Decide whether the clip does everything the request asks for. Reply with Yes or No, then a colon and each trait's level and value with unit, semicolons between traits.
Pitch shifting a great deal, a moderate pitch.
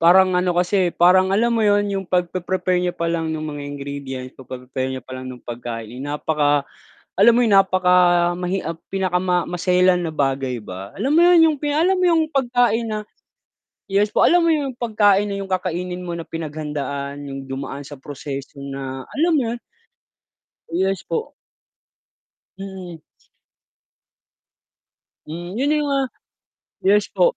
Yes: wide, 6.3 semitones; medium, 180 Hz